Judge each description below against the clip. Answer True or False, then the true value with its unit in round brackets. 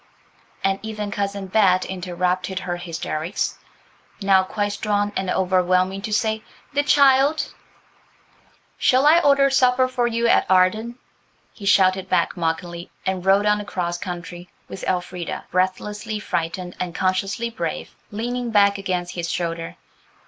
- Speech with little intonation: False (3.2 semitones)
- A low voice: False (195 Hz)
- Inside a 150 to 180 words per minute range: False (135 wpm)